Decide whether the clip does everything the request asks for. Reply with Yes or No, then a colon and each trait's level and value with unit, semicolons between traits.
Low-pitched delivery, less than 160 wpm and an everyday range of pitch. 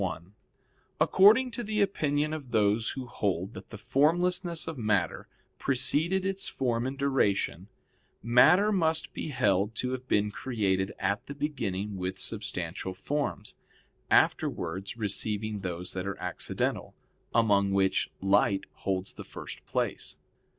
No: low, 110 Hz; slow, 135 wpm; wide, 7.2 semitones